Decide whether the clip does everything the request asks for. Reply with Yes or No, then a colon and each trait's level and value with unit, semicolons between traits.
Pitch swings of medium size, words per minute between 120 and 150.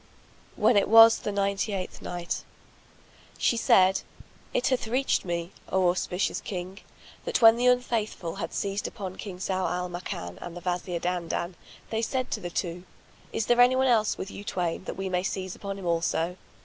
No: average, 3.8 semitones; average, 180 wpm